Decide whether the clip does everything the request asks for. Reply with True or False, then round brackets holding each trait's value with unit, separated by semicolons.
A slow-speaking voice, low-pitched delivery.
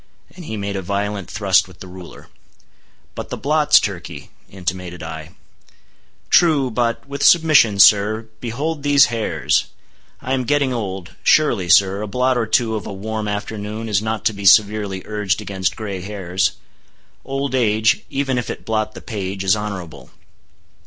False (150 wpm; 105 Hz)